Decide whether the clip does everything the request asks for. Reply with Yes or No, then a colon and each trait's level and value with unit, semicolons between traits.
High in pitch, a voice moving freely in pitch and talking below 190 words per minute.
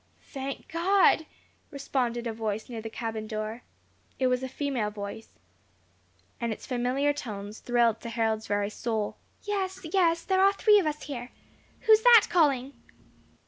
Yes: very high, 250 Hz; wide, 6.6 semitones; average, 155 wpm